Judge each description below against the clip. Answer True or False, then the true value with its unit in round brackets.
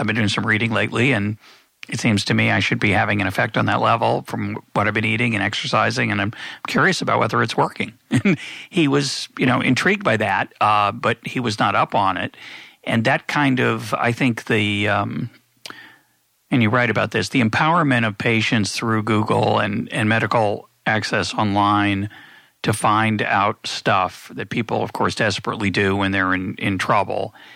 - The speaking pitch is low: True (110 Hz)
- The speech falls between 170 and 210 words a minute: True (190 wpm)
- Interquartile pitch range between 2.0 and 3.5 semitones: True (2.5 semitones)